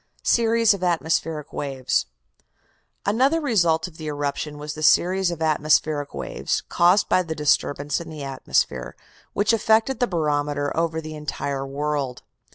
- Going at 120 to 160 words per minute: Yes, average, 145 wpm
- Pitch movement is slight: No, average, 4.0 semitones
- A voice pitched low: No, medium, 155 Hz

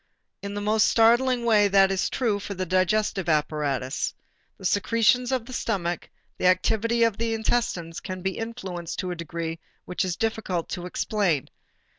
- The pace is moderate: Yes, average, 170 wpm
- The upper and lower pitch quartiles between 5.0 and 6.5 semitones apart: No, average, 4.3 semitones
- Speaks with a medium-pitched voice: No, high, 195 Hz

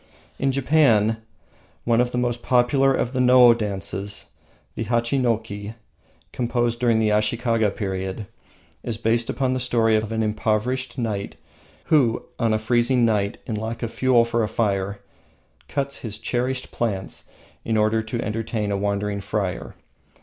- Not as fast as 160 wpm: Yes, average, 150 wpm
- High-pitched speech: No, low, 115 Hz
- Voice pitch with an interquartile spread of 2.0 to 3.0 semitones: Yes, narrow, 2.5 semitones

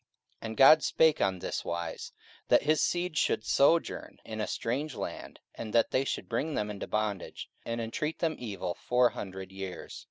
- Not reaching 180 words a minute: No, average, 185 wpm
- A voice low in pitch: Yes, low, 115 Hz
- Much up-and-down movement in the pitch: Yes, wide, 6.8 semitones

